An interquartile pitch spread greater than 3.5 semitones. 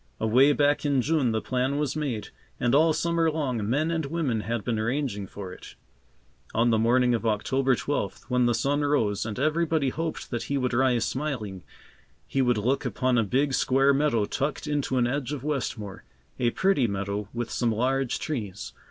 Yes: average, 4.0 semitones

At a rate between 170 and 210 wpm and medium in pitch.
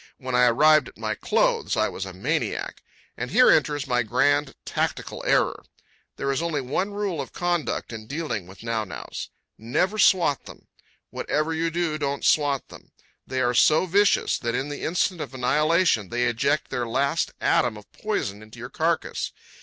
Yes: average, 175 wpm; medium, 145 Hz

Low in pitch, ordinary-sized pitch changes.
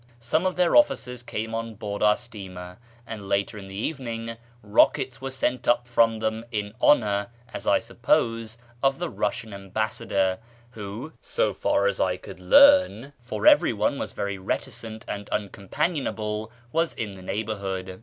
Yes: low, 110 Hz; average, 3.6 semitones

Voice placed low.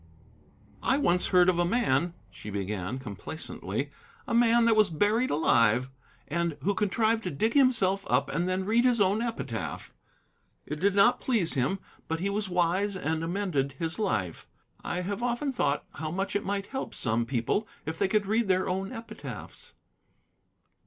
No: medium, 185 Hz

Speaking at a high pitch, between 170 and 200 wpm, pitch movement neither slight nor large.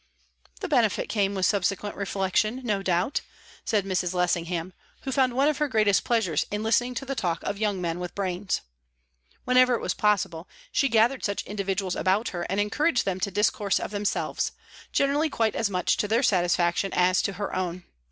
Yes: high, 200 Hz; average, 185 wpm; average, 3.9 semitones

